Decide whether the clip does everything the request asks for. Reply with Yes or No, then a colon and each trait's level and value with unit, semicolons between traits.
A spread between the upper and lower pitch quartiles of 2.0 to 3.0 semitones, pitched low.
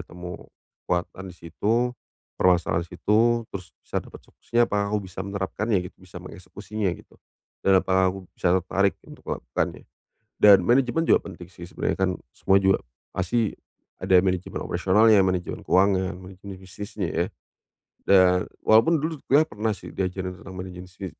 Yes: narrow, 2.4 semitones; very low, 95 Hz